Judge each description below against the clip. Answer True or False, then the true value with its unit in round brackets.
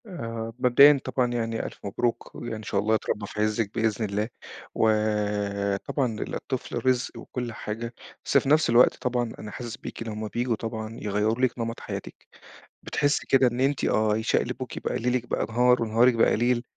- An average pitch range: False (2.3 semitones)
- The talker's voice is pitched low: True (115 Hz)